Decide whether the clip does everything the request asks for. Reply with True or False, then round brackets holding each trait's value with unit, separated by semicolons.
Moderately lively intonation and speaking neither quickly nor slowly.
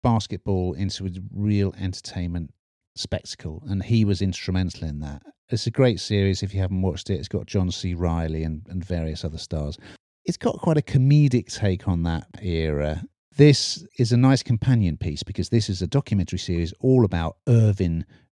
True (4.7 semitones; 180 wpm)